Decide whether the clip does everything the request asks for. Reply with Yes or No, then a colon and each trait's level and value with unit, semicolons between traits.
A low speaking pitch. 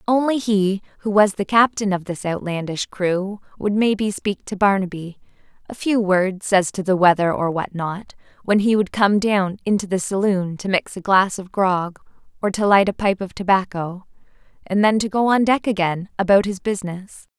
No: high, 195 Hz